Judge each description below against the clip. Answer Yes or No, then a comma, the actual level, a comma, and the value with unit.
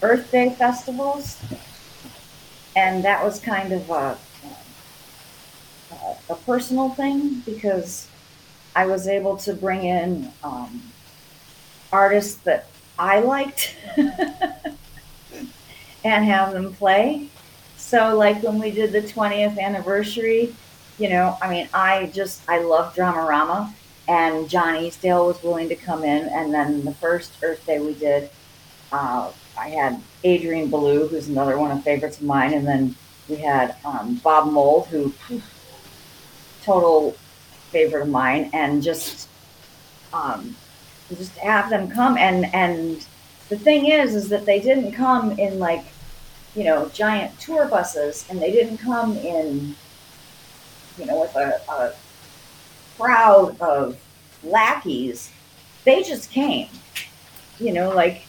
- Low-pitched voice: No, high, 190 Hz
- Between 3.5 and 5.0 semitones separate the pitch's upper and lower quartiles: No, wide, 5.5 semitones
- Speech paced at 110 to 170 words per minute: Yes, slow, 135 wpm